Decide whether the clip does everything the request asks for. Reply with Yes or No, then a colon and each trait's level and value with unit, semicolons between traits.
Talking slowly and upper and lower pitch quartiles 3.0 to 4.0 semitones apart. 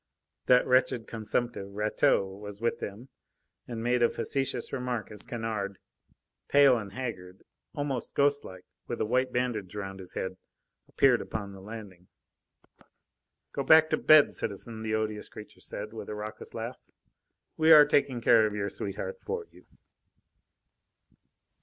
No: average, 145 wpm; average, 3.7 semitones